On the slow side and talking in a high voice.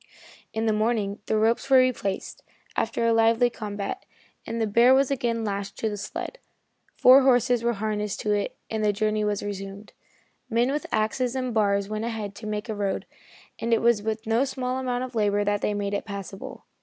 No: average, 200 wpm; high, 220 Hz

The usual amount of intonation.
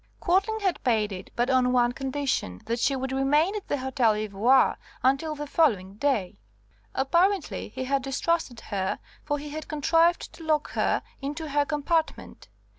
Yes: average, 4.3 semitones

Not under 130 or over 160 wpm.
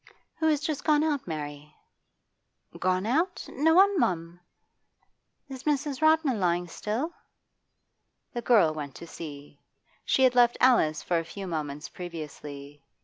Yes: average, 140 wpm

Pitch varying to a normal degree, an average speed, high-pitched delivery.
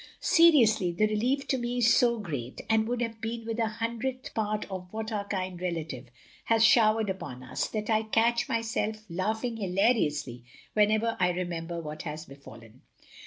Yes: average, 4.6 semitones; average, 170 wpm; high, 215 Hz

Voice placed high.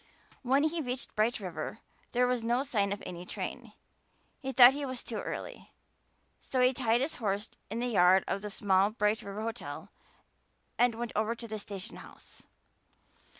Yes: high, 230 Hz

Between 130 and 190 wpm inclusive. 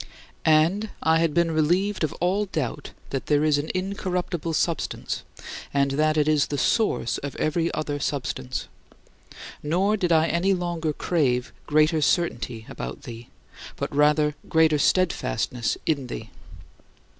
Yes: average, 145 wpm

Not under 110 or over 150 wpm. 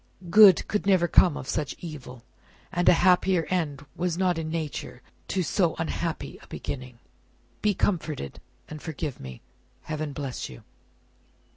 Yes: average, 140 wpm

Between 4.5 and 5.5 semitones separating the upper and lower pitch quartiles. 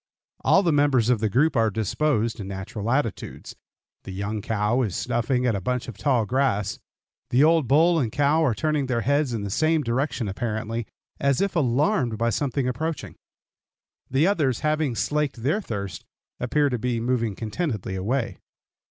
Yes: average, 4.9 semitones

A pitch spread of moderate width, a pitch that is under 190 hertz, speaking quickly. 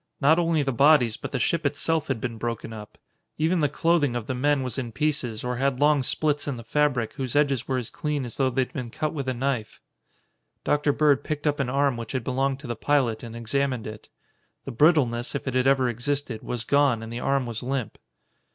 Yes: average, 3.4 semitones; low, 135 Hz; fast, 230 wpm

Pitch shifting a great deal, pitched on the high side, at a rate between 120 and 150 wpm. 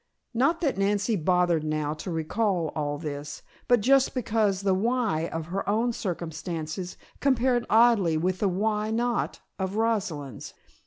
Yes: wide, 5.9 semitones; high, 195 Hz; average, 145 wpm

